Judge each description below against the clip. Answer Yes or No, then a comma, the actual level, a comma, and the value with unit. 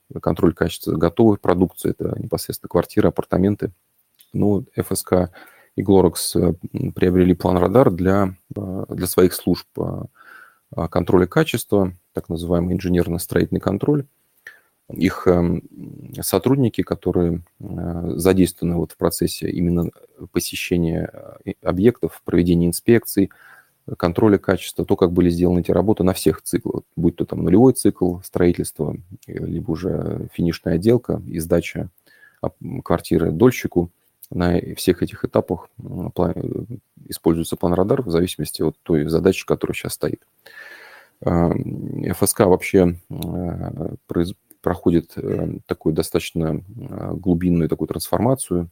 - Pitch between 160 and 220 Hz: No, very low, 90 Hz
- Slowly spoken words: Yes, slow, 105 wpm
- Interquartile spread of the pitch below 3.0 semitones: Yes, narrow, 2.6 semitones